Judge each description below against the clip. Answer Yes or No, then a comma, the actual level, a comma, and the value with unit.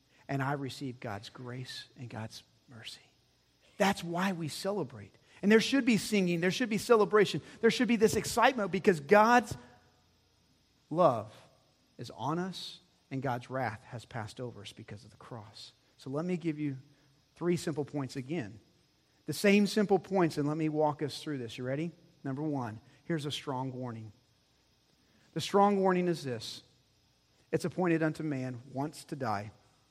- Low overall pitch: No, medium, 145 Hz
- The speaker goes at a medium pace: Yes, average, 165 wpm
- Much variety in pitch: Yes, wide, 6.4 semitones